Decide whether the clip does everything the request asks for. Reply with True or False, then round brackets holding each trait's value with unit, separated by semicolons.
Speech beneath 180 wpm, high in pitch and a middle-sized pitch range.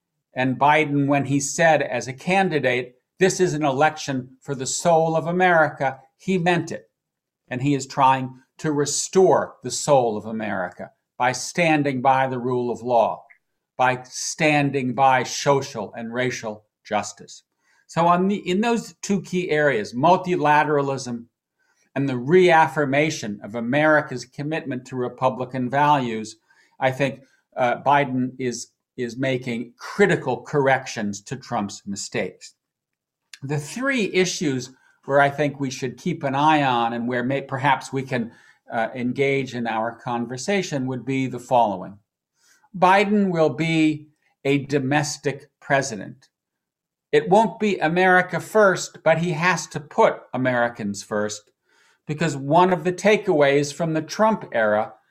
False (140 wpm; 140 Hz; 4.1 semitones)